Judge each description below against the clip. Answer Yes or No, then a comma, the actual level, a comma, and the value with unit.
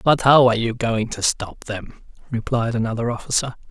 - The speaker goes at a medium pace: Yes, average, 180 wpm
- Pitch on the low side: Yes, low, 115 Hz